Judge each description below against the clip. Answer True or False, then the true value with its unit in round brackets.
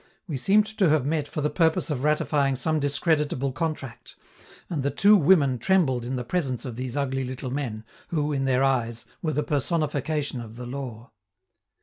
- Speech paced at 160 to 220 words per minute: True (185 wpm)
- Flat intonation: False (3.4 semitones)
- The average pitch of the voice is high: False (140 Hz)